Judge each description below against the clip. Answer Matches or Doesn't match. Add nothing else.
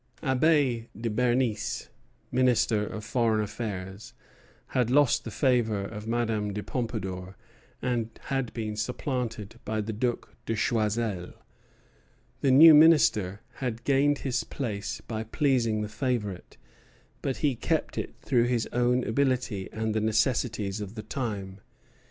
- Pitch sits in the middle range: Doesn't match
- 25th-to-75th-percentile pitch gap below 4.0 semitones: Matches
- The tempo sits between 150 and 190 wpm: Doesn't match